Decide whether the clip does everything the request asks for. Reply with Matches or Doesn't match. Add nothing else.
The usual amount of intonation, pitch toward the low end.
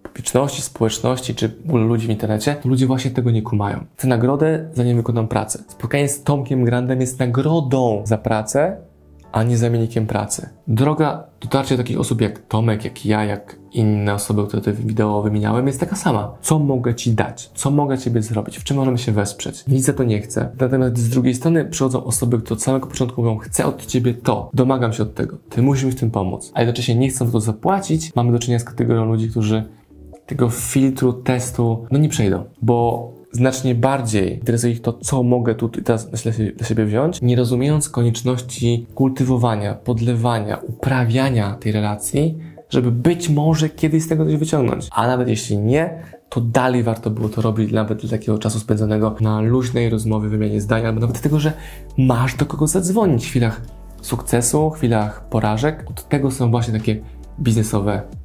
Matches